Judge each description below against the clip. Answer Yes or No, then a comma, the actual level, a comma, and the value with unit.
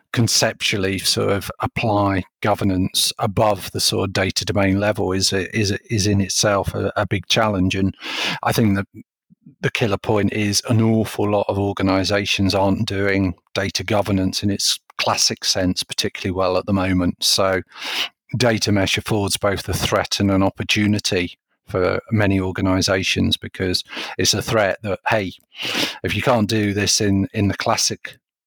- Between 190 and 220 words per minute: No, average, 160 wpm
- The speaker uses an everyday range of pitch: No, narrow, 2.2 semitones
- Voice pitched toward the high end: No, low, 100 Hz